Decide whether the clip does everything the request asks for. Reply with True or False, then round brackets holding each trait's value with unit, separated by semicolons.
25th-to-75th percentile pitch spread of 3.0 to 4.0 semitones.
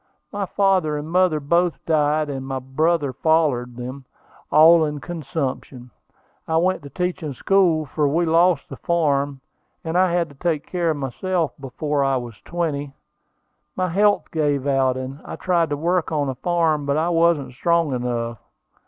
True (3.7 semitones)